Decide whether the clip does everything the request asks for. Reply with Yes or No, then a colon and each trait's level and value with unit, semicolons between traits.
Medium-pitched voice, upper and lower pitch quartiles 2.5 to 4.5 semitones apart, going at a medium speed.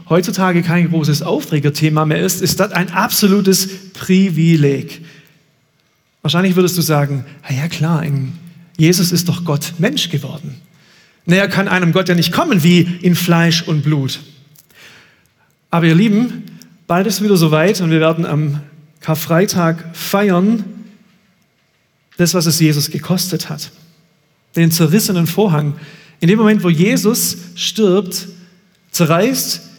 Yes: medium, 170 Hz; average, 3.4 semitones; average, 135 wpm